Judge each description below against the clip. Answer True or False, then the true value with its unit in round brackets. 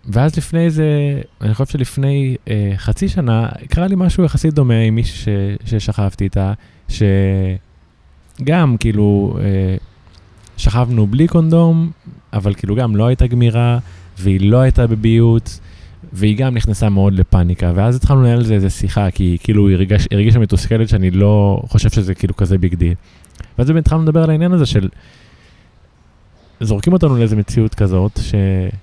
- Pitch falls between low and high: False (105 Hz)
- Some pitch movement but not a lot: True (4.1 semitones)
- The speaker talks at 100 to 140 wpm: False (150 wpm)